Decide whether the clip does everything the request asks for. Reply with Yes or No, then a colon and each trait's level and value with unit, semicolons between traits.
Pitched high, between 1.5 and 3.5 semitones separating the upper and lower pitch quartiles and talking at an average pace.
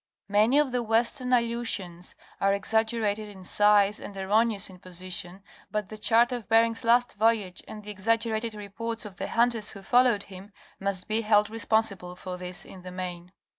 Yes: high, 210 Hz; average, 3.0 semitones; average, 170 wpm